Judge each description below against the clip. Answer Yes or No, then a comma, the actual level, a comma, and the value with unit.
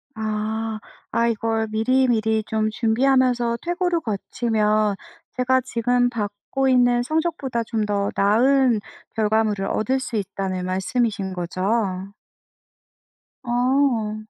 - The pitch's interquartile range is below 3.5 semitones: Yes, average, 2.9 semitones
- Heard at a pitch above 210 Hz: Yes, high, 225 Hz